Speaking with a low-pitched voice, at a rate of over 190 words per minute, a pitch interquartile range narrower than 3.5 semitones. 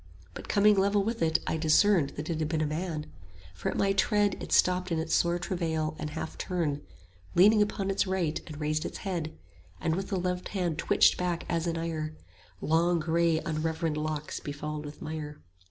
No: medium, 165 Hz; average, 200 wpm; average, 2.9 semitones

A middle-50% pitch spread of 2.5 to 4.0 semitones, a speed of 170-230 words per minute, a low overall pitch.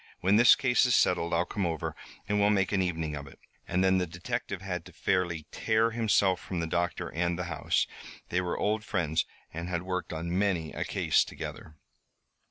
Yes: average, 3.0 semitones; average, 200 wpm; very low, 90 Hz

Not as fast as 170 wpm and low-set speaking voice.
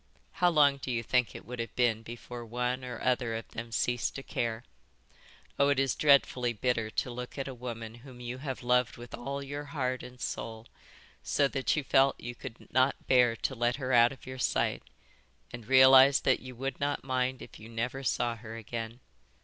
No: fast, 205 wpm; low, 125 Hz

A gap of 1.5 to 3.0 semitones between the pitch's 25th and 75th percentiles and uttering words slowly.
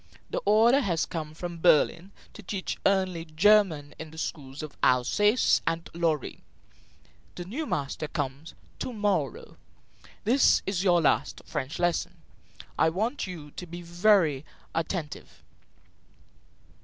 No: average, 4.3 semitones; slow, 130 wpm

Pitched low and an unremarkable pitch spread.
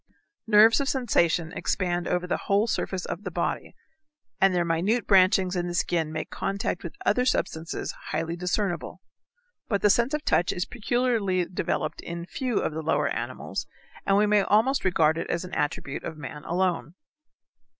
No: medium, 185 Hz; average, 3.6 semitones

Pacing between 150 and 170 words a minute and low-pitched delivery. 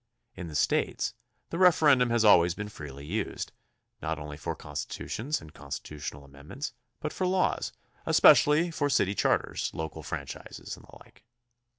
Yes: average, 155 wpm; low, 100 Hz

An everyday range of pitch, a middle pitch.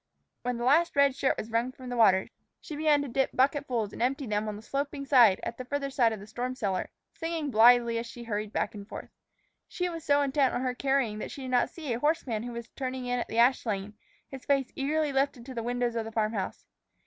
No: average, 3.4 semitones; very high, 250 Hz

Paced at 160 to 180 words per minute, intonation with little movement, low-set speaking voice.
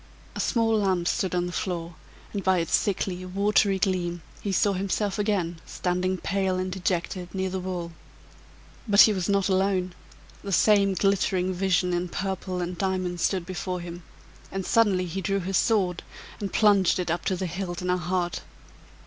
No: average, 175 wpm; narrow, 1.7 semitones; medium, 185 Hz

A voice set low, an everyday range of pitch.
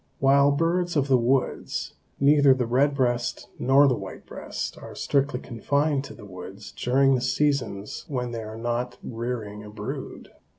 Yes: low, 125 Hz; average, 3.1 semitones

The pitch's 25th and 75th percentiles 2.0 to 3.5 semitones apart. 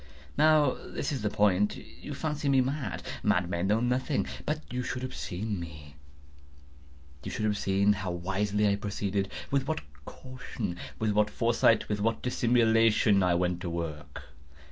No: average, 5.0 semitones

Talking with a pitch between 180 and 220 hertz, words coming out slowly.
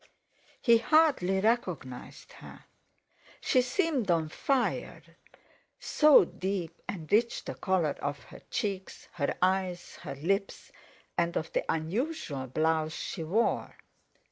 Yes: medium, 185 Hz; slow, 115 wpm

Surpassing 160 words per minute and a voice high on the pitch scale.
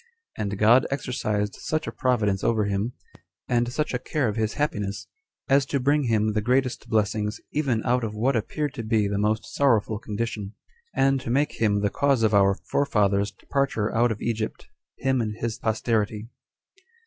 No: average, 175 wpm; low, 115 Hz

